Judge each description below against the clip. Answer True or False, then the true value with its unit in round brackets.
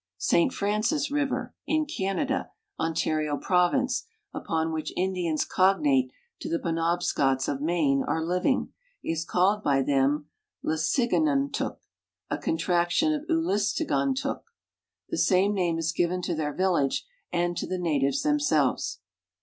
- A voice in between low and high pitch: True (175 Hz)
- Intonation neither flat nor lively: False (6.1 semitones)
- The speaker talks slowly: True (125 wpm)